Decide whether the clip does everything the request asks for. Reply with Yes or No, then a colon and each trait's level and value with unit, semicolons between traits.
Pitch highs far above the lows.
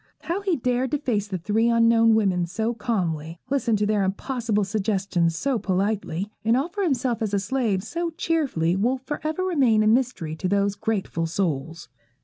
No: average, 5.0 semitones